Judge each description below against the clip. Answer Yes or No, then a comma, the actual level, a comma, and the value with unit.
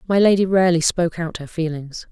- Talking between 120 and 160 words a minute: No, average, 200 wpm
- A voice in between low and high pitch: Yes, medium, 170 Hz